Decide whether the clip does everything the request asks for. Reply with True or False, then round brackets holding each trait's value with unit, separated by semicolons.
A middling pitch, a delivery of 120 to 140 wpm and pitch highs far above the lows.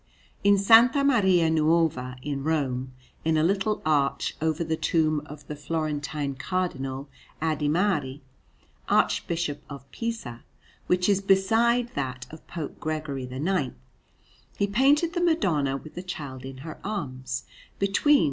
True (155 Hz; 135 wpm; 5.7 semitones)